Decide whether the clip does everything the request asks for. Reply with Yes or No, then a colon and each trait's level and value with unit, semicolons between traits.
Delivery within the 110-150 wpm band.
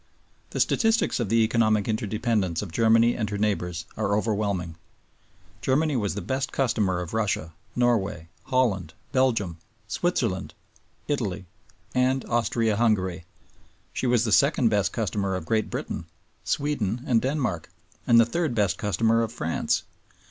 Yes: average, 140 wpm